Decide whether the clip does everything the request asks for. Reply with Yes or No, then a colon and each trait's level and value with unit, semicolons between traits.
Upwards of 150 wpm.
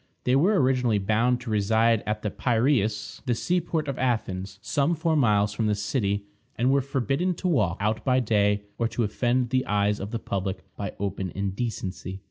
Yes: average, 190 wpm